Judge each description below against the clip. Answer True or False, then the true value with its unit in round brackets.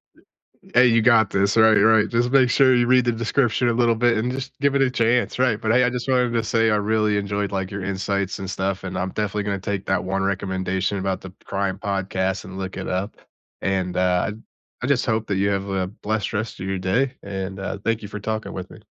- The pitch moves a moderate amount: True (3.4 semitones)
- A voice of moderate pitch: False (105 Hz)